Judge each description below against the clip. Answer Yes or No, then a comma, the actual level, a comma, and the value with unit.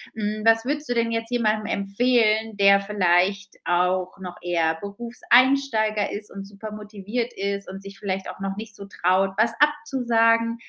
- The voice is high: Yes, high, 210 Hz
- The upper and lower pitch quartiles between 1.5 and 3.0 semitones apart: Yes, average, 2.7 semitones